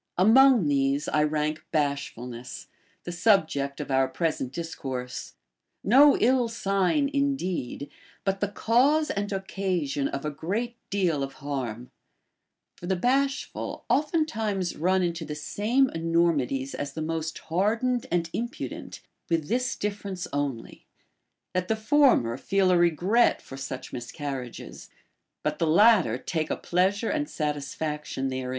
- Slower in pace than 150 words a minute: Yes, slow, 135 wpm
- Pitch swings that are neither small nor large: No, wide, 7.1 semitones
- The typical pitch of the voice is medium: Yes, medium, 170 Hz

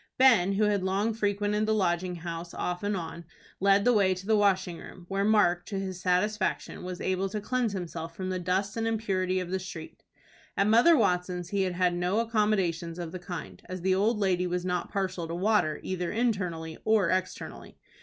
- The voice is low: No, medium, 185 Hz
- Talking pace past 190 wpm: Yes, average, 200 wpm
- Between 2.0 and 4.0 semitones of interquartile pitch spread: Yes, average, 2.7 semitones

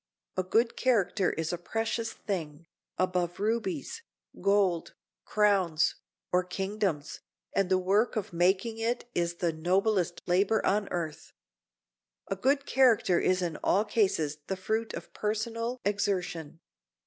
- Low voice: No, high, 195 Hz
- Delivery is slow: Yes, slow, 130 wpm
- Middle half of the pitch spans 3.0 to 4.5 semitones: Yes, average, 3.9 semitones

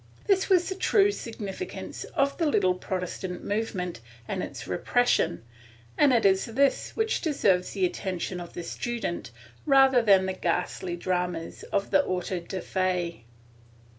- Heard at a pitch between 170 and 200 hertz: Yes, high, 190 Hz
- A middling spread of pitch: No, wide, 7.0 semitones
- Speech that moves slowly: No, average, 145 wpm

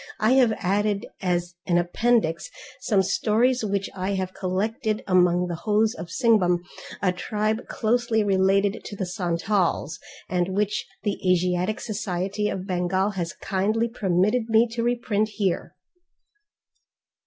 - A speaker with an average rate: No, slow, 130 wpm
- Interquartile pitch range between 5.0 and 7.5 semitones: No, average, 3.2 semitones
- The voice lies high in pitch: Yes, high, 200 Hz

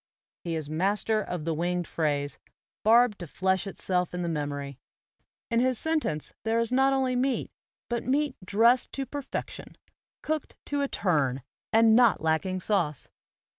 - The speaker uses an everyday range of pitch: No, wide, 7.4 semitones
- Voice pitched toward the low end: No, high, 200 Hz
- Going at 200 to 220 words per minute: No, average, 155 wpm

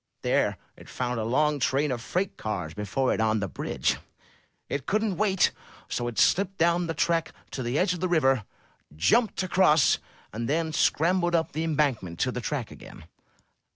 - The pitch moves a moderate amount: No, wide, 6.2 semitones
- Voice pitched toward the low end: No, medium, 150 Hz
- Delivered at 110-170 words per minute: No, average, 180 wpm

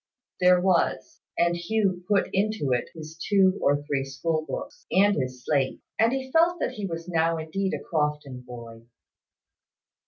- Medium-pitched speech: Yes, medium, 165 Hz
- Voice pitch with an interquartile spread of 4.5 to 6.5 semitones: Yes, average, 5.2 semitones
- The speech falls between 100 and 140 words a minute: No, average, 155 wpm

